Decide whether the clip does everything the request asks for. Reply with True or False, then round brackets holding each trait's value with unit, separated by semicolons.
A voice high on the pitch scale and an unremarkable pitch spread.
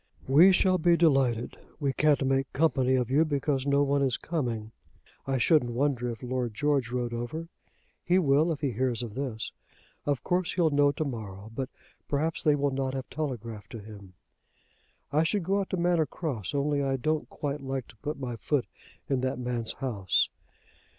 False (135 Hz; 3.7 semitones)